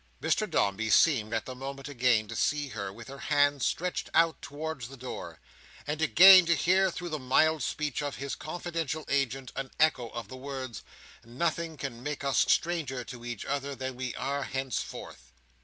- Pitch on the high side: No, medium, 140 Hz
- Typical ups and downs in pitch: Yes, average, 3.9 semitones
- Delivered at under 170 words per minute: No, average, 180 wpm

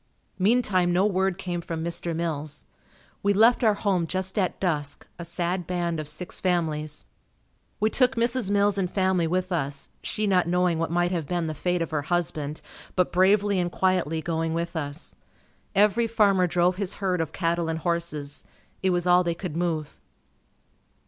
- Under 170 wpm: No, average, 175 wpm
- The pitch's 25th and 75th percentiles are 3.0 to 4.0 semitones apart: No, narrow, 2.5 semitones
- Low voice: No, medium, 175 Hz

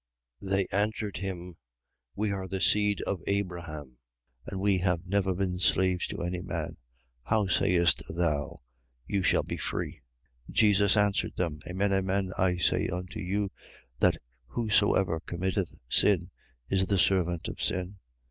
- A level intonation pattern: Yes, narrow, 2.1 semitones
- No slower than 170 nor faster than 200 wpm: No, average, 145 wpm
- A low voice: Yes, very low, 95 Hz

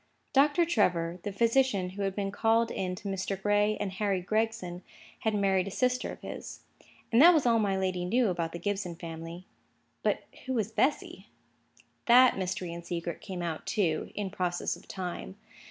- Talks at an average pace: Yes, average, 180 wpm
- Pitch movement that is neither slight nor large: Yes, average, 3.8 semitones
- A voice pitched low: No, high, 195 Hz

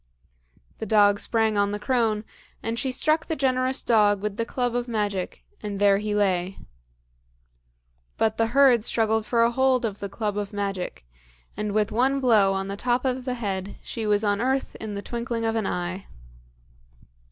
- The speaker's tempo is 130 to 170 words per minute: No, average, 185 wpm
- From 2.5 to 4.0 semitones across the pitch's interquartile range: Yes, average, 3.1 semitones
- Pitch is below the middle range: No, high, 220 Hz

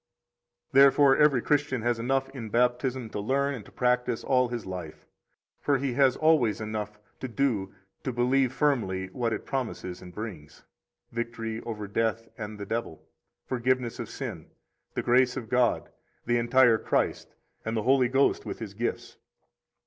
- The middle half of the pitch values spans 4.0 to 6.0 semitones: No, average, 3.1 semitones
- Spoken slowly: No, average, 165 wpm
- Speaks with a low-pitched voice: Yes, low, 120 Hz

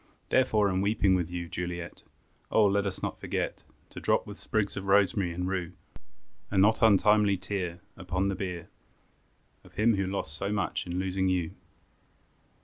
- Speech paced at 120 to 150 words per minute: No, average, 165 wpm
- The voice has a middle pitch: No, very low, 95 Hz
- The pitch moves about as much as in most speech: No, narrow, 2.1 semitones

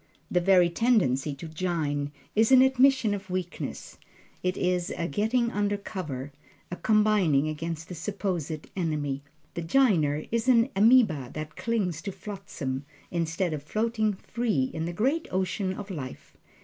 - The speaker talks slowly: No, average, 150 wpm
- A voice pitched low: No, medium, 180 Hz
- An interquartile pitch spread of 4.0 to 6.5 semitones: Yes, wide, 5.4 semitones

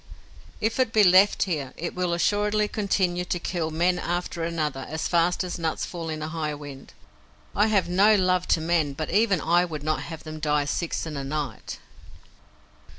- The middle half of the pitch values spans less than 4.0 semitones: Yes, average, 2.9 semitones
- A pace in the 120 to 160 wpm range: No, average, 195 wpm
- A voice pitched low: No, medium, 170 Hz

